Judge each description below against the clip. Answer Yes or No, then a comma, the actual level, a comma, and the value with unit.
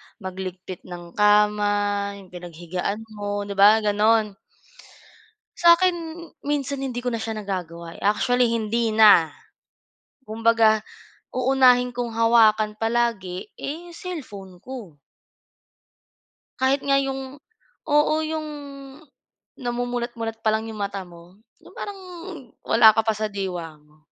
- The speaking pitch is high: Yes, high, 220 Hz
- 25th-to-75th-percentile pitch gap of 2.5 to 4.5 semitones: Yes, average, 3.8 semitones